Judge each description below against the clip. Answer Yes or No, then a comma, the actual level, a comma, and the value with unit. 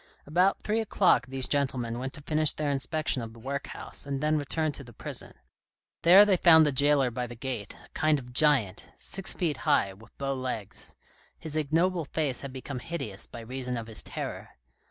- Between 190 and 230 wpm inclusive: Yes, average, 195 wpm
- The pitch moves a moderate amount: Yes, average, 3.9 semitones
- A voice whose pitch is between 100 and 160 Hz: Yes, medium, 140 Hz